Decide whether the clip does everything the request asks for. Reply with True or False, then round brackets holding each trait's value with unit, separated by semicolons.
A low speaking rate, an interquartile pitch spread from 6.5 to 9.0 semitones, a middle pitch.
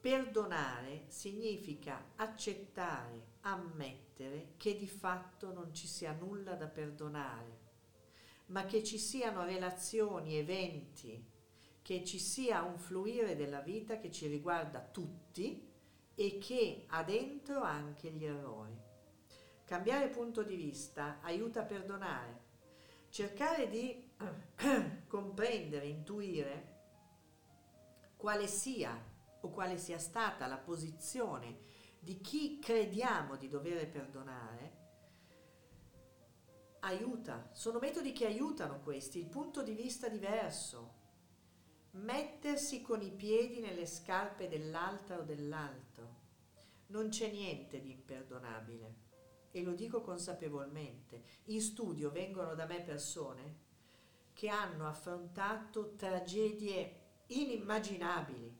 True (105 wpm; 7.7 semitones; 175 Hz)